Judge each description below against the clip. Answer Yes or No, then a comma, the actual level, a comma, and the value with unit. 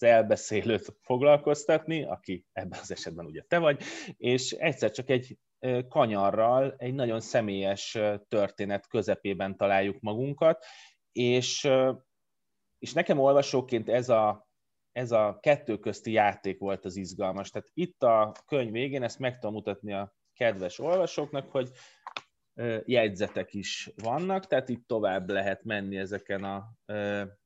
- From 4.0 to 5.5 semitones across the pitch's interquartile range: Yes, average, 4.6 semitones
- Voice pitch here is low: Yes, low, 115 Hz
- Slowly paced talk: No, average, 125 wpm